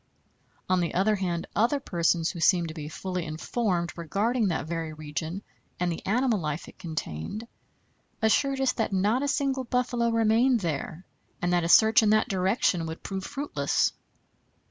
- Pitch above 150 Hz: Yes, high, 190 Hz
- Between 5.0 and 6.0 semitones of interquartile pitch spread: Yes, wide, 5.5 semitones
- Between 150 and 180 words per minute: Yes, average, 165 wpm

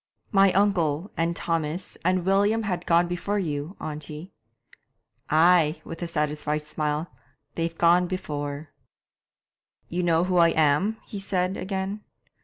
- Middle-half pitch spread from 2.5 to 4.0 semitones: Yes, average, 3.5 semitones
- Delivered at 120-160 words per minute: Yes, slow, 135 wpm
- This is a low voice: No, medium, 170 Hz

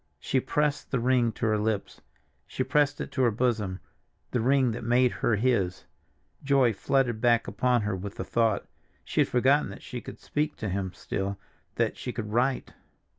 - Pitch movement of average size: Yes, average, 3.4 semitones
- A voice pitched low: Yes, low, 120 Hz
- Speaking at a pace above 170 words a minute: Yes, average, 180 wpm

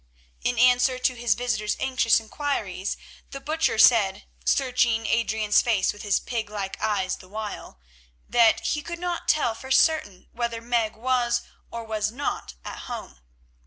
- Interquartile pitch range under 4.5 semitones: Yes, average, 3.0 semitones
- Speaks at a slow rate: No, average, 155 wpm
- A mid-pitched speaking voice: No, high, 230 Hz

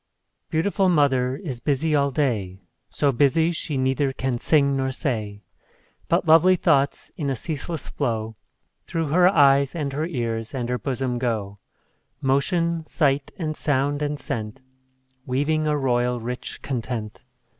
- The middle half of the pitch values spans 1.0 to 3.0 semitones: No, average, 3.8 semitones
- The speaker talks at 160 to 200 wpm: No, average, 145 wpm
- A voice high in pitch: No, medium, 140 Hz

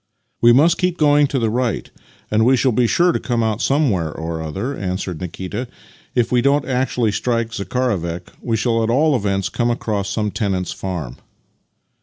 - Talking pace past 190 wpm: Yes, average, 200 wpm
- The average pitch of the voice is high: No, low, 115 Hz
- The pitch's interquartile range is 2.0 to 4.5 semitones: No, average, 4.9 semitones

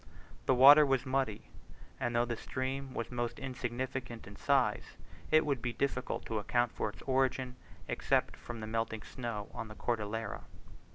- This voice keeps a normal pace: Yes, average, 165 wpm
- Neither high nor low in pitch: No, low, 120 Hz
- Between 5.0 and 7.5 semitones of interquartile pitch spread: No, narrow, 2.5 semitones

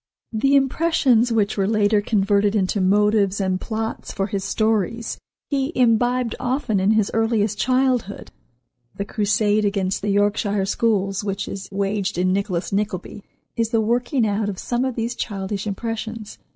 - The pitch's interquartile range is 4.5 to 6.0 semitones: No, narrow, 2.5 semitones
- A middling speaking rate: Yes, average, 150 wpm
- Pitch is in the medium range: No, high, 210 Hz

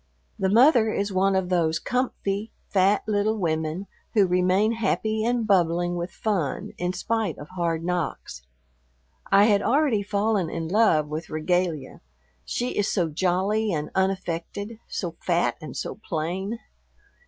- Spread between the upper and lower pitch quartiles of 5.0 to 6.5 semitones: No, average, 3.9 semitones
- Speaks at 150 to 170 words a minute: No, average, 140 wpm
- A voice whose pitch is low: No, high, 190 Hz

